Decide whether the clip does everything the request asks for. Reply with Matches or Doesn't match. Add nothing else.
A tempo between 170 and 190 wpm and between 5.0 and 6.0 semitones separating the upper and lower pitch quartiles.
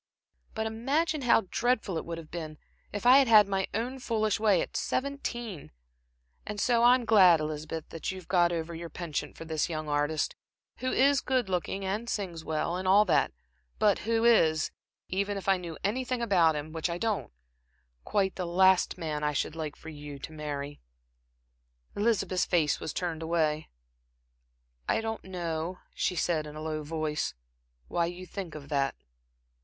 Matches